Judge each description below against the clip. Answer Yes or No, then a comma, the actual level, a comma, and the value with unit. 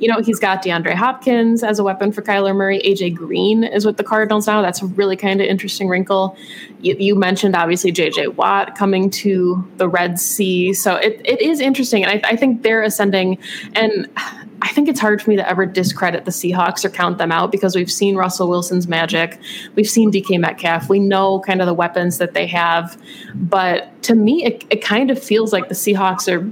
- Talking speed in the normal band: No, fast, 215 wpm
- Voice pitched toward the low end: No, high, 195 Hz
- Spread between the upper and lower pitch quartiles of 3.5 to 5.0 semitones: No, average, 2.8 semitones